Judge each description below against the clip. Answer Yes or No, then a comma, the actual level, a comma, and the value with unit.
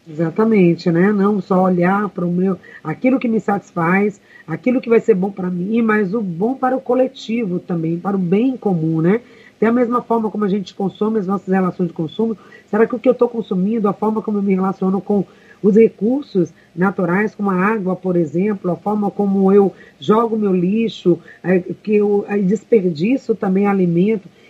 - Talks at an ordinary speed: No, fast, 195 wpm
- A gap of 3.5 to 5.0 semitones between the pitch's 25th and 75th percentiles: No, average, 3.1 semitones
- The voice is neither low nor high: No, high, 200 Hz